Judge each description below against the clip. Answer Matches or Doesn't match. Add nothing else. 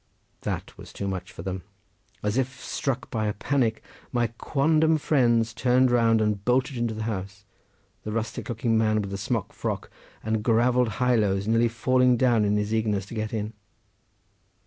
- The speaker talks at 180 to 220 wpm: Doesn't match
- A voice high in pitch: Doesn't match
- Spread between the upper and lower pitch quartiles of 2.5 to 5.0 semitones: Matches